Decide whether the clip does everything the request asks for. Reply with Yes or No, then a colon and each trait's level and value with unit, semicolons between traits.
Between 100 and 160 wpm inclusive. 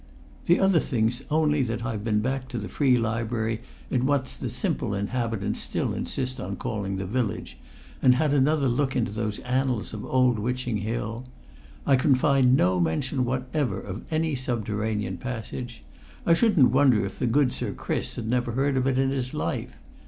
No: average, 175 wpm